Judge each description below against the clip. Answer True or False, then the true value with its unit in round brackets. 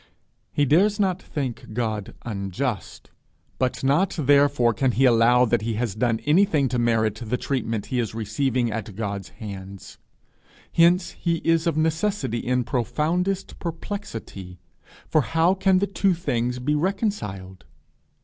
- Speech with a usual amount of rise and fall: False (6.7 semitones)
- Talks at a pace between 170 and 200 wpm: False (140 wpm)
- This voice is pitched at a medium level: False (125 Hz)